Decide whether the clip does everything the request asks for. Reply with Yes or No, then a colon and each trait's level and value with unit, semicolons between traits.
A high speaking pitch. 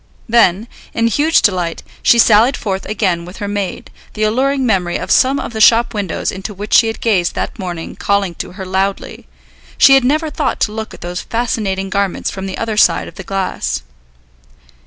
Yes: high, 205 Hz